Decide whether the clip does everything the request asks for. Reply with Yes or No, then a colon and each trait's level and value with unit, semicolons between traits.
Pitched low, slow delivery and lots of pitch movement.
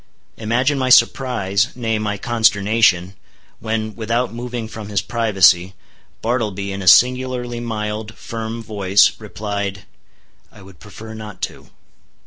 No: low, 110 Hz; slow, 120 wpm; narrow, 2.6 semitones